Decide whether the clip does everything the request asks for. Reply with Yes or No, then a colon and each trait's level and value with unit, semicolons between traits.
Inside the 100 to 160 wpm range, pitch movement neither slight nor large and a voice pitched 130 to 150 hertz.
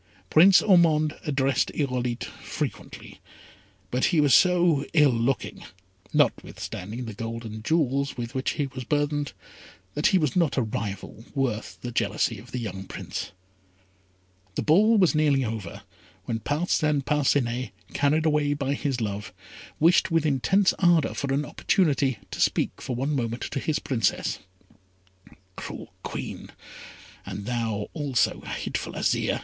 Yes: average, 140 wpm; average, 4.5 semitones; low, 135 Hz